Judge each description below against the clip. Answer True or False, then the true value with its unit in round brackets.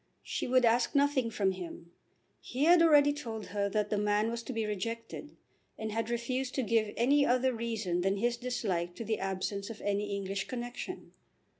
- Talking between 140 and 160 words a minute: False (185 wpm)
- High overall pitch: True (225 Hz)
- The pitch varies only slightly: False (3.7 semitones)